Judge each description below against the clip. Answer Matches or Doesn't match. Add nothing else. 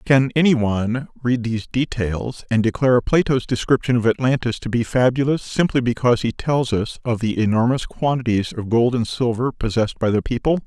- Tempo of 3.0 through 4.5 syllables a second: Doesn't match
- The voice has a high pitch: Doesn't match